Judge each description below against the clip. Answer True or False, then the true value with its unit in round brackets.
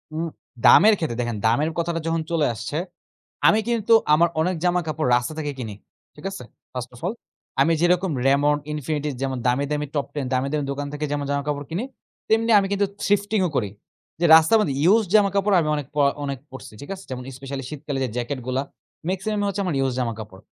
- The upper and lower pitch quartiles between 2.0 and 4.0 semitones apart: False (5.0 semitones)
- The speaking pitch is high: False (150 Hz)